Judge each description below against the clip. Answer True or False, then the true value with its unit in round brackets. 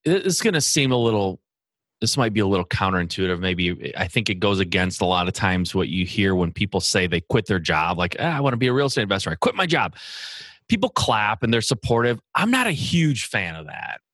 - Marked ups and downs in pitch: True (6.5 semitones)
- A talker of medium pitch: False (105 Hz)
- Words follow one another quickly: True (245 wpm)